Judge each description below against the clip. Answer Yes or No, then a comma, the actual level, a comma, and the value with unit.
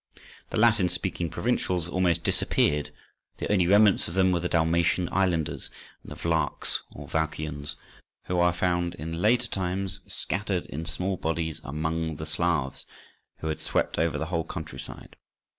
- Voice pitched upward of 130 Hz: No, very low, 85 Hz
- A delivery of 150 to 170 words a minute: Yes, average, 160 wpm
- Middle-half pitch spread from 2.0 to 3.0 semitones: Yes, narrow, 2.5 semitones